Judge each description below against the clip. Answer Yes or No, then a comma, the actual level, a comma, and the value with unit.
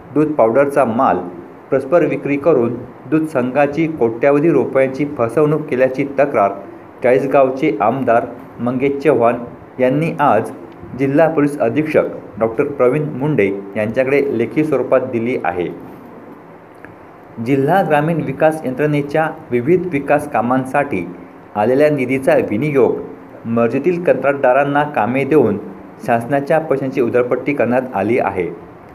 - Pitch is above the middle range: No, medium, 140 Hz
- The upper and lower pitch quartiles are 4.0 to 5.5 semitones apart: No, average, 3.3 semitones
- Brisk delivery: No, average, 105 wpm